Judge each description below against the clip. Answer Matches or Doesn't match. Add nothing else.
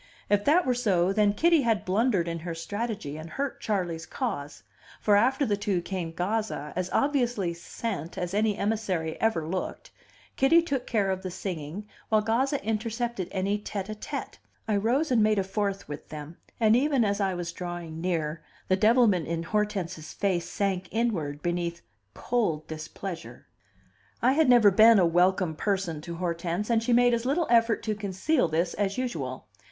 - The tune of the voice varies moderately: Matches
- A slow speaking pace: Doesn't match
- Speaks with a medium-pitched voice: Doesn't match